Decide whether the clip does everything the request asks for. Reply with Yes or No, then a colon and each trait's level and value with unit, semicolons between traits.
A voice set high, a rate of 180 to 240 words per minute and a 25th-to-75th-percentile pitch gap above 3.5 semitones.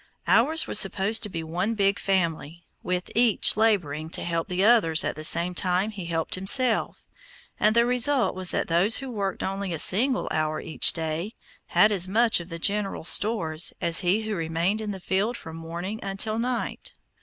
Yes: high, 195 Hz; average, 190 wpm; average, 4.5 semitones